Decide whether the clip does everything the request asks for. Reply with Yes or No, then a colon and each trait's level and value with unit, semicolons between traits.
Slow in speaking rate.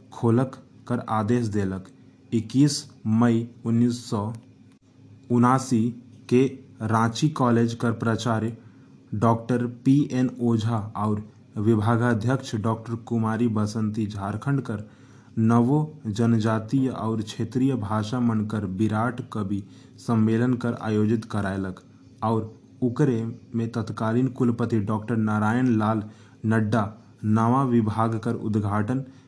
Yes: slow, 100 wpm